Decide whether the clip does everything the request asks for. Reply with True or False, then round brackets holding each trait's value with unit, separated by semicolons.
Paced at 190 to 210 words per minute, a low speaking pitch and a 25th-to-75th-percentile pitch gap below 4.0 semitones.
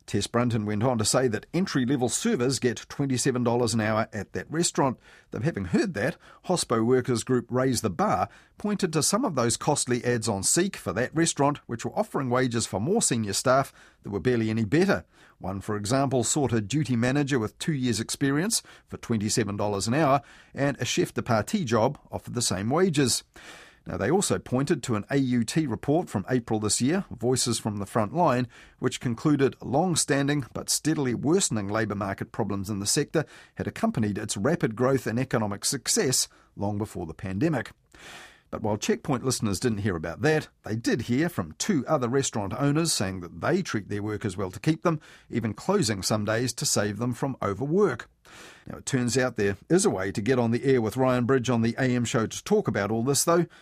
False (200 wpm; 125 Hz; 4.5 semitones)